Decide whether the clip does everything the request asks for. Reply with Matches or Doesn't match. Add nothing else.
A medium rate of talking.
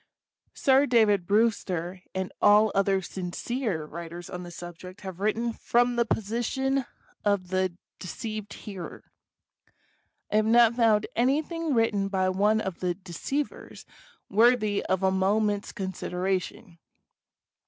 Doesn't match